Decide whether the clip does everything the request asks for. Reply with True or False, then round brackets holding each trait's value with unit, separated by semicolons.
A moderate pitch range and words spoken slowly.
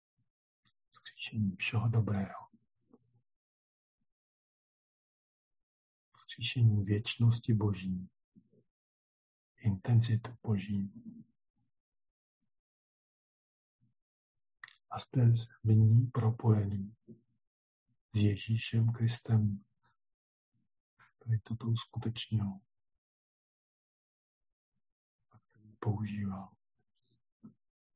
True (3.2 semitones; 40 wpm)